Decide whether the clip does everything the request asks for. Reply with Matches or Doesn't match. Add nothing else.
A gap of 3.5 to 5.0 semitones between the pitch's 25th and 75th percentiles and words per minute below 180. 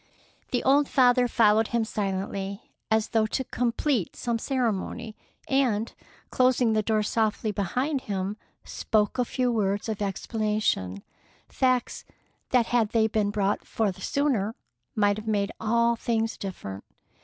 Doesn't match